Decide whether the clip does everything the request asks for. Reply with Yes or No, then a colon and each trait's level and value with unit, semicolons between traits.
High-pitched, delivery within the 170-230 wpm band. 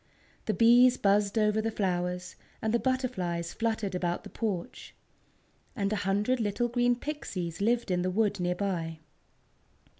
No: high, 205 Hz; average, 150 wpm